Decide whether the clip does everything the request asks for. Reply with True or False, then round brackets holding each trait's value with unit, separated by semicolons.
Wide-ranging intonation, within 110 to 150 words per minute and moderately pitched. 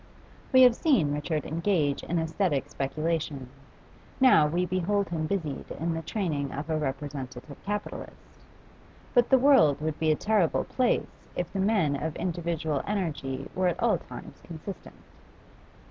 False (4.9 semitones; 145 wpm; 165 Hz)